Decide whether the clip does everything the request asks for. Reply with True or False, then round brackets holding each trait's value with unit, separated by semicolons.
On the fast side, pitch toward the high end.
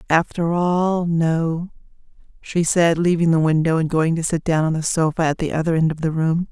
False (210 wpm; 165 Hz)